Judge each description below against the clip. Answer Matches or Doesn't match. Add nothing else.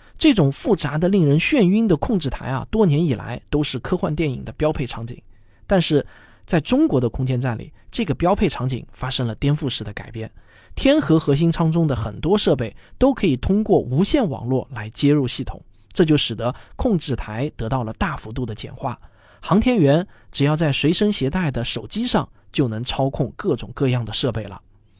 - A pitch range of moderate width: Doesn't match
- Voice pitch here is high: Doesn't match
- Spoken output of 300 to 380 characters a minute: Doesn't match